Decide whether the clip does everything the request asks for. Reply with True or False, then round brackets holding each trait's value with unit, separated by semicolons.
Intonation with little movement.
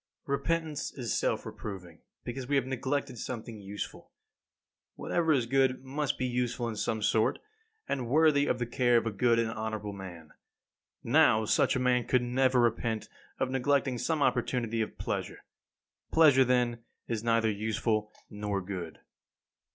False (3.3 semitones)